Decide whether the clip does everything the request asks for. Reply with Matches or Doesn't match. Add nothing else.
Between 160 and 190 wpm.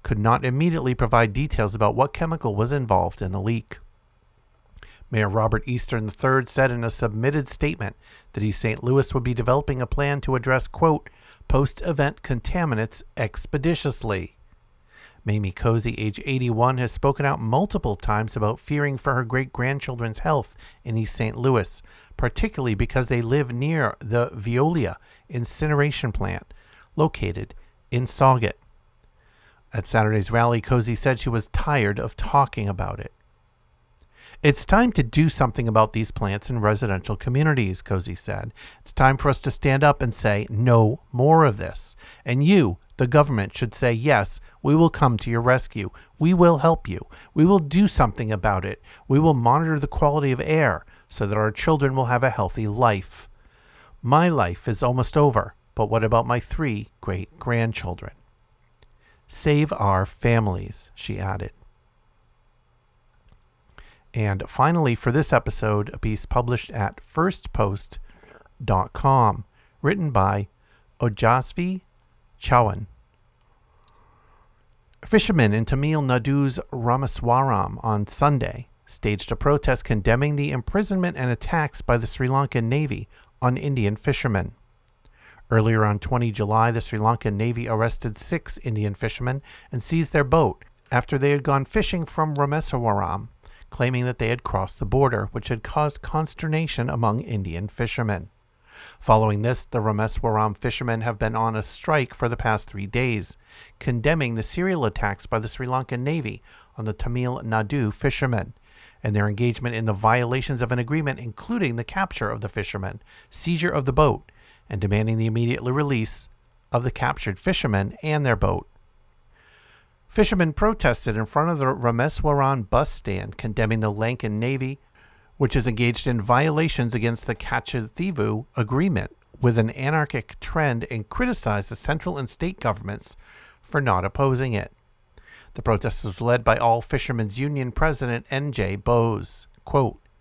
Doesn't match